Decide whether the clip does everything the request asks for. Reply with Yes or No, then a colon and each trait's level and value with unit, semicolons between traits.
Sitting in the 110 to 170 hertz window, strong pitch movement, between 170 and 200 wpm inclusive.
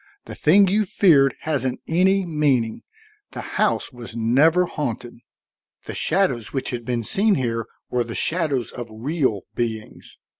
No: low, 135 Hz; wide, 6.3 semitones; average, 145 wpm